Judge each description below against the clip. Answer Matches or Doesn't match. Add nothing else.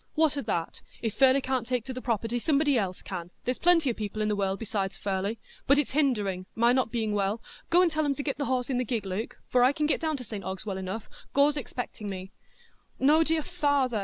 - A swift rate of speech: Matches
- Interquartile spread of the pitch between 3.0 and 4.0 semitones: Doesn't match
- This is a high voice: Matches